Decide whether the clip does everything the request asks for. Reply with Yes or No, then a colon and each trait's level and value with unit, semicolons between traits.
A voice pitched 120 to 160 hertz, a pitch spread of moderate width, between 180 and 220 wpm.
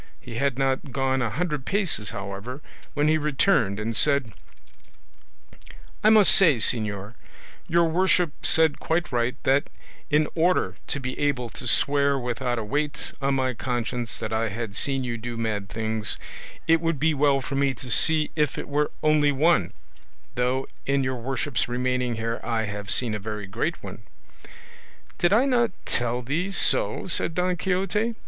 No: low, 135 Hz; average, 4.8 semitones; average, 170 wpm